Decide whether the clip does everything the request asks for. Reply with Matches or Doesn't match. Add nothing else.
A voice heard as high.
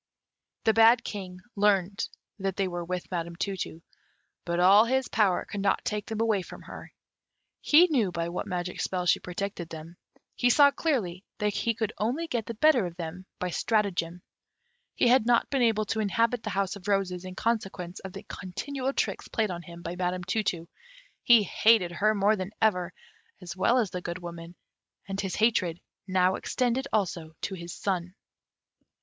Matches